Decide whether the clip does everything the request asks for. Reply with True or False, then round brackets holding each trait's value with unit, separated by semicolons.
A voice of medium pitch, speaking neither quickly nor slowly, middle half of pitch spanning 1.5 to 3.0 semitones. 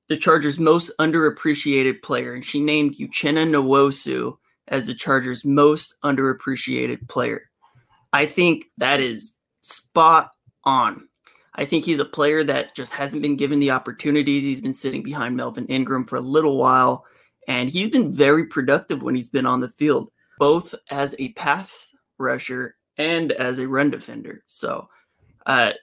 True (145 Hz; 155 wpm; 2.5 semitones)